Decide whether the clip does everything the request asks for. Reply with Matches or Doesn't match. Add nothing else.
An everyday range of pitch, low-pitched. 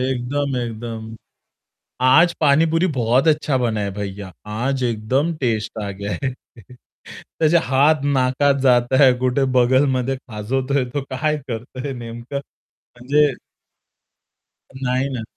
Matches